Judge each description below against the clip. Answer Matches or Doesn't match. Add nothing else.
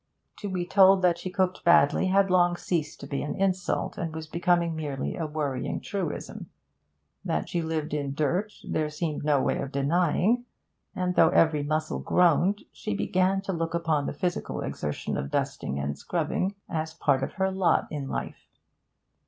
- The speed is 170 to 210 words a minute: Matches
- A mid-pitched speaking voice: Matches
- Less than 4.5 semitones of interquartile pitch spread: Matches